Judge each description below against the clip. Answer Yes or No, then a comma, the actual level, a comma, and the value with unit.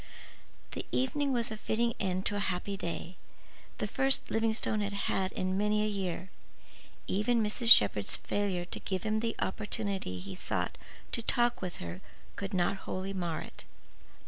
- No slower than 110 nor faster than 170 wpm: Yes, average, 160 wpm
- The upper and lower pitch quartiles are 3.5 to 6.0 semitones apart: No, average, 3.1 semitones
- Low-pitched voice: No, high, 200 Hz